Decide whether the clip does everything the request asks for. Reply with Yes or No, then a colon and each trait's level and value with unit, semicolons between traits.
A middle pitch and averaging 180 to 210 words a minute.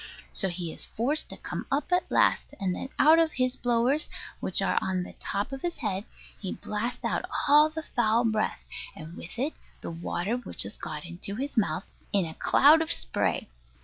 No: high, 230 Hz; average, 200 wpm